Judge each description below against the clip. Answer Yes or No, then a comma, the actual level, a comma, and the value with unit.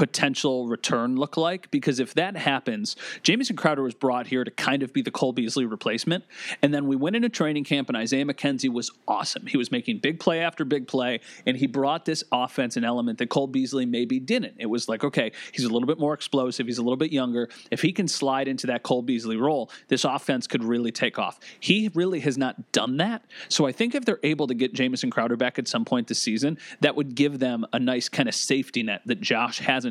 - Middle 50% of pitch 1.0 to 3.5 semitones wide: No, average, 4.1 semitones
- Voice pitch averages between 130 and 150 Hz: Yes, medium, 140 Hz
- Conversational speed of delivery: No, fast, 235 wpm